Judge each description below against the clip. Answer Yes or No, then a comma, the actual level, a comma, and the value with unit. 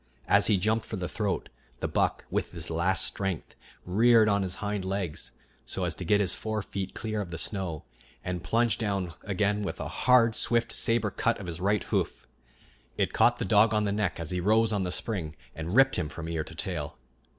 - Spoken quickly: Yes, fast, 215 wpm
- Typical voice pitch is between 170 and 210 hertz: No, low, 100 Hz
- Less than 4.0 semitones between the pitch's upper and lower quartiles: Yes, average, 3.5 semitones